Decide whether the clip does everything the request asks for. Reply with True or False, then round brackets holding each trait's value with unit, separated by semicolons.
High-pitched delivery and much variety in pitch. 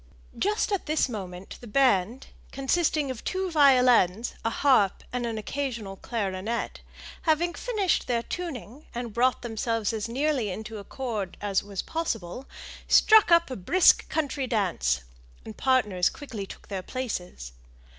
True (240 Hz; 5.8 semitones)